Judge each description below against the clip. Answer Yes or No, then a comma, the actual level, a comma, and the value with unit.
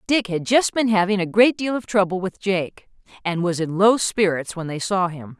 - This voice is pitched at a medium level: No, high, 195 Hz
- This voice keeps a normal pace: No, fast, 235 wpm